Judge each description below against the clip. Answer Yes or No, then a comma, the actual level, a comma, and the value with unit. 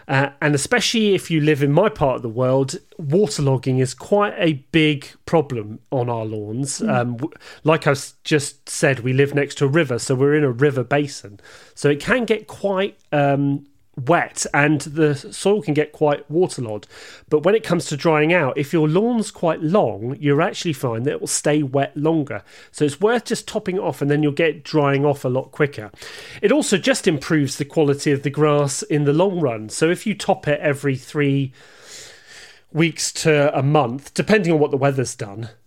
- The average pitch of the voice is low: No, medium, 150 Hz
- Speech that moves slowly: No, average, 200 wpm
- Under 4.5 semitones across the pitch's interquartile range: Yes, average, 3.6 semitones